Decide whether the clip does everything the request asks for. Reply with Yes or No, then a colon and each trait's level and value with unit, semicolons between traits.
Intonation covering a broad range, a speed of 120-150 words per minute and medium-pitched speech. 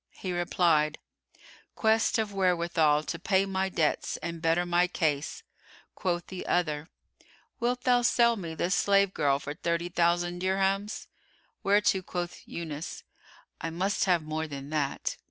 No: average, 3.2 semitones; average, 140 wpm; medium, 175 Hz